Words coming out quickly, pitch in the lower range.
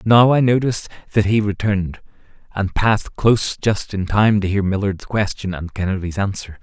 No: average, 170 wpm; low, 100 Hz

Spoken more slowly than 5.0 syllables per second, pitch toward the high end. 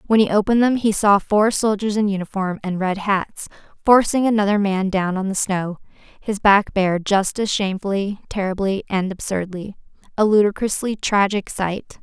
No: 5.1 syllables/s; high, 200 Hz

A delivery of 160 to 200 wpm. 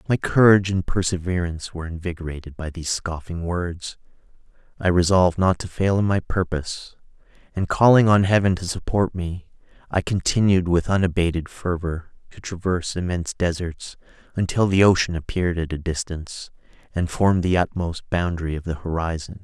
No: average, 150 wpm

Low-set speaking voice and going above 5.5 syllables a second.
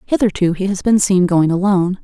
No: high, 190 Hz; 5.7 syllables/s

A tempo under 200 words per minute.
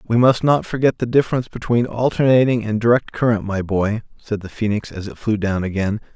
No: fast, 205 wpm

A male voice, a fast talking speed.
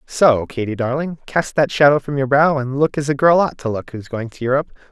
Yes: male; fast, 255 wpm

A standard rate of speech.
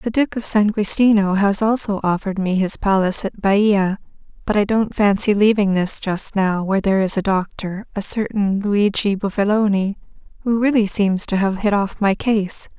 Yes: average, 185 wpm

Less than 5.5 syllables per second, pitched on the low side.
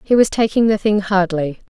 No: 5.3 syllables/s; high, 200 Hz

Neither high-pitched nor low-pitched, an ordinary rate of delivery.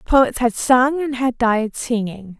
No: high, 240 Hz; average, 175 wpm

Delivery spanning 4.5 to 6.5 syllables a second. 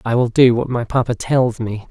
Yes: 5.0 syllables/s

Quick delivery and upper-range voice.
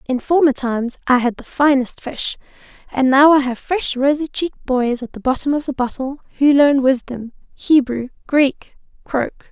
No: average, 170 wpm; very high, 270 Hz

